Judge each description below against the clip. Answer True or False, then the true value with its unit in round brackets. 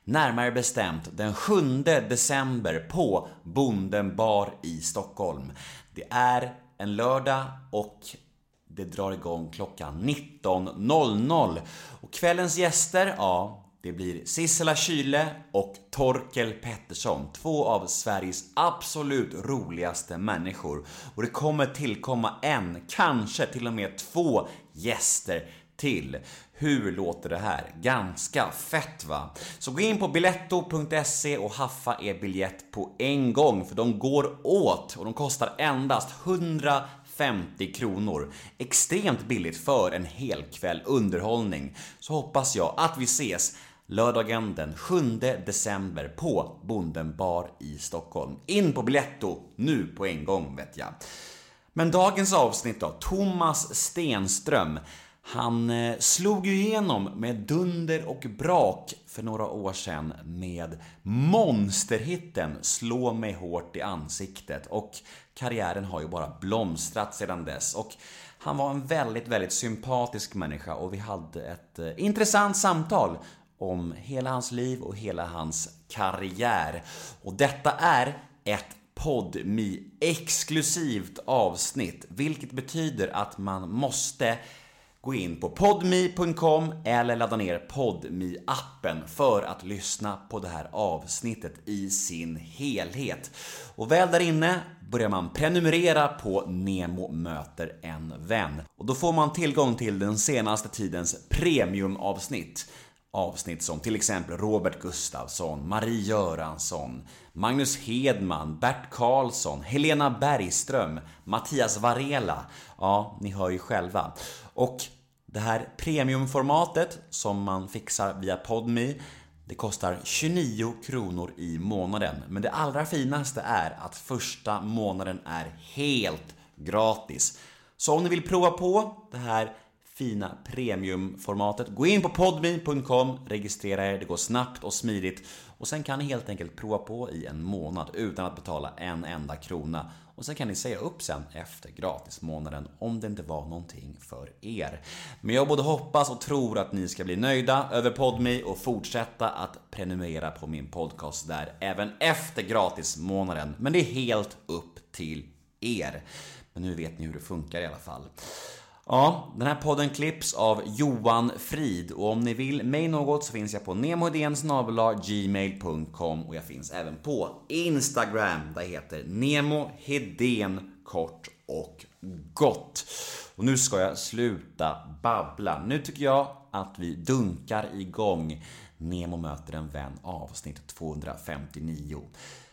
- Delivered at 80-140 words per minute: True (135 wpm)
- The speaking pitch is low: True (110 Hz)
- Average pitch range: False (7.7 semitones)